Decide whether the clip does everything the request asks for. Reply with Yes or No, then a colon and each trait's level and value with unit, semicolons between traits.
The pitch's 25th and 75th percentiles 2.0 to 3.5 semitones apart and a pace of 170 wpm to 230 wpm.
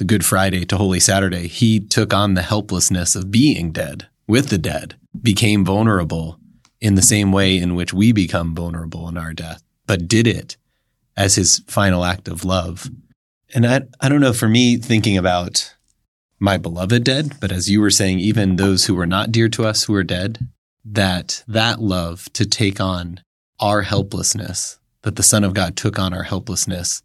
Yes: average, 3.2 semitones; average, 190 wpm